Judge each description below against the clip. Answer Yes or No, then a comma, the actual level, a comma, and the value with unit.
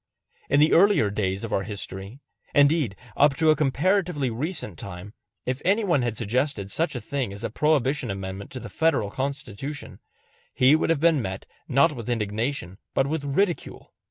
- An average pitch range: No, wide, 6.6 semitones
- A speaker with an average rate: Yes, average, 175 wpm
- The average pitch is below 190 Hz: Yes, low, 135 Hz